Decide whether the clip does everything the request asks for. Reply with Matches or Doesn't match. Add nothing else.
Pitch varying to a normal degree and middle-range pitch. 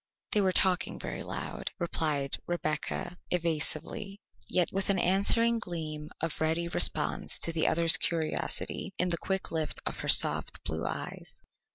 Matches